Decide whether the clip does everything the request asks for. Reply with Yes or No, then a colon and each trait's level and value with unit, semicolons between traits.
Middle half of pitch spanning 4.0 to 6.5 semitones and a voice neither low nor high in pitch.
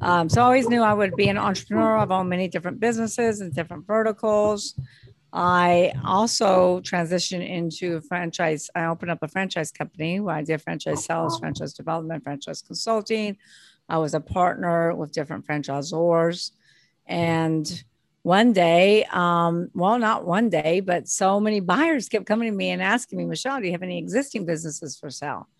Yes: average, 4.3 semitones; medium, 175 Hz